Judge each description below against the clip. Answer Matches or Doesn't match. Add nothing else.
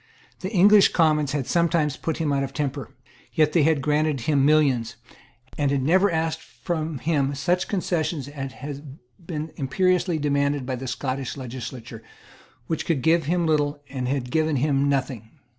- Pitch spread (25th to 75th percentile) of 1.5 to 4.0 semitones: Matches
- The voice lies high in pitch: Doesn't match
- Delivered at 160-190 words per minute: Matches